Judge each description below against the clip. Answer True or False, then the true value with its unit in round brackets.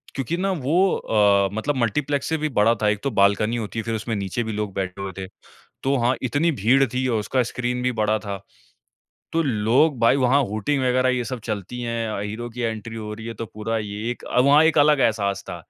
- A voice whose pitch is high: False (115 Hz)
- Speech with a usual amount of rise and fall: True (3.4 semitones)